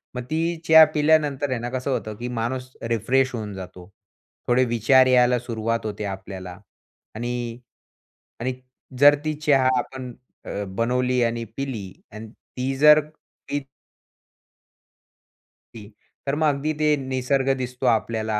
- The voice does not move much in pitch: No, average, 3.1 semitones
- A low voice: Yes, low, 125 Hz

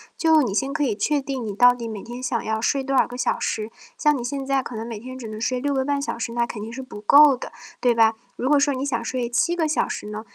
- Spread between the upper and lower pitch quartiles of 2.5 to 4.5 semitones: Yes, average, 3.3 semitones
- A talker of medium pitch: No, very high, 250 Hz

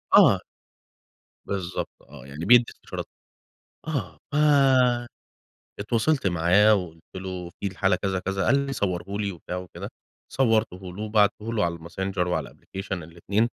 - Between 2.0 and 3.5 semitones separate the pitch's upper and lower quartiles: No, average, 3.9 semitones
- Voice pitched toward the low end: Yes, very low, 95 Hz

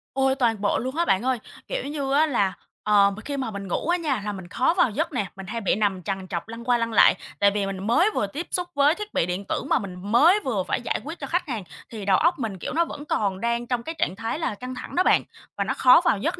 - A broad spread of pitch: Yes, wide, 6.5 semitones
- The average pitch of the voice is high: Yes, high, 235 Hz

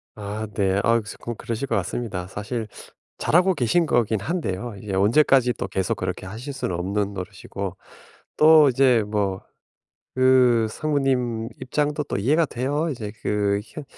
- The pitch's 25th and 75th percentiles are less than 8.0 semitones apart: Yes, average, 5.2 semitones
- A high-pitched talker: No, low, 115 Hz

